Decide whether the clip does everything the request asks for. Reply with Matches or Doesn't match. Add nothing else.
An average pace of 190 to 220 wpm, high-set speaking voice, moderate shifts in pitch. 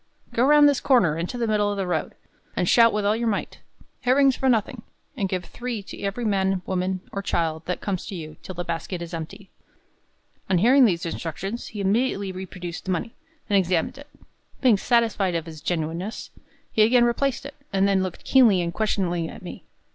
Matches